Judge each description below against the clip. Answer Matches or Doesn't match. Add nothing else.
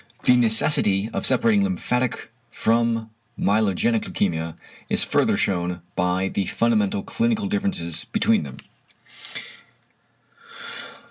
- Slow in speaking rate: Matches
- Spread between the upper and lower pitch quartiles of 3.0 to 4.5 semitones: Doesn't match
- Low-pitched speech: Matches